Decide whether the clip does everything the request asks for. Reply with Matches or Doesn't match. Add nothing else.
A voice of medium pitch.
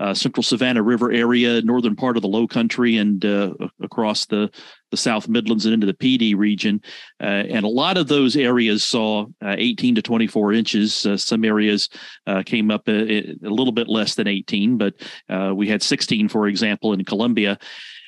Doesn't match